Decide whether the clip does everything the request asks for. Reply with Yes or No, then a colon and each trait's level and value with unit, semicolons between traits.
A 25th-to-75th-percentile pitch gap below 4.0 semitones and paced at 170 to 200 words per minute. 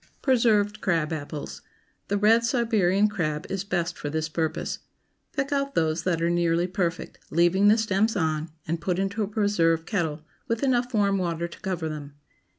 No: average, 4.4 semitones; average, 175 wpm